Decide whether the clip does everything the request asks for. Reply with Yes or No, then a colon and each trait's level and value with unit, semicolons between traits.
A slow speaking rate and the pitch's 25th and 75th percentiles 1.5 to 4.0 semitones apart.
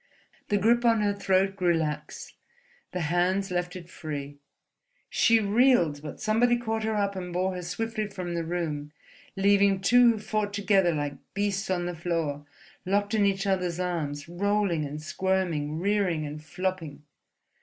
No: average, 160 wpm; average, 3.5 semitones